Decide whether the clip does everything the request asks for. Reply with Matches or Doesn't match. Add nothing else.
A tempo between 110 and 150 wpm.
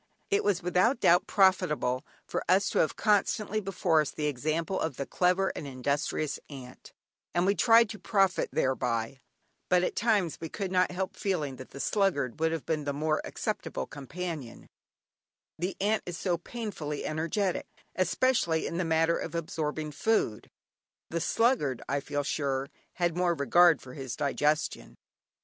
Doesn't match